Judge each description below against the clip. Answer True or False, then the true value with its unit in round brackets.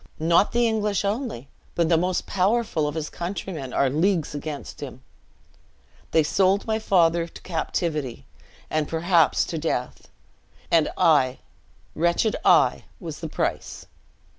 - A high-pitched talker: False (170 Hz)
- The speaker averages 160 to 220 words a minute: False (135 wpm)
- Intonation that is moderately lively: True (4.2 semitones)